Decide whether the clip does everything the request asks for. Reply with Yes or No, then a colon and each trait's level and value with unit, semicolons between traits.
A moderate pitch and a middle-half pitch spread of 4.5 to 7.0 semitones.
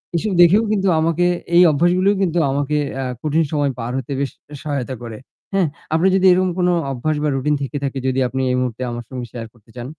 Yes: medium, 145 Hz; average, 5.2 semitones